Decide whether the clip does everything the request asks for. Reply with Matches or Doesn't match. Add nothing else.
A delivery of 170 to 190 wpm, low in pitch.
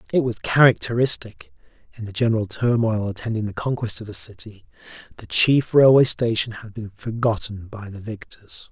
Doesn't match